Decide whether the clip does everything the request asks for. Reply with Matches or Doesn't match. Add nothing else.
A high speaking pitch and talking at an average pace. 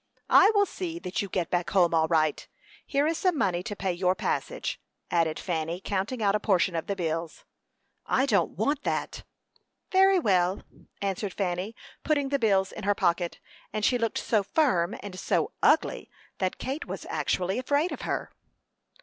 Matches